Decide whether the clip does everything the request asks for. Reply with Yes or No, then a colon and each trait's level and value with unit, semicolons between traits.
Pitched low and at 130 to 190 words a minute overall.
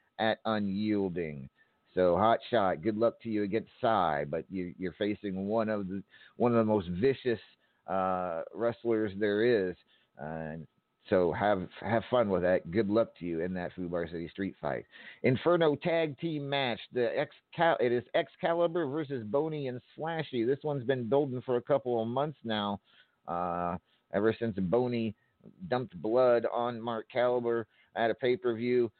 Yes: low, 115 Hz; average, 175 wpm